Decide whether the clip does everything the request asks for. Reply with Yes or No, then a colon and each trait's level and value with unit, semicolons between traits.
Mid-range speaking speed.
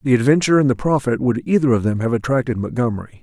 No: fast, 225 wpm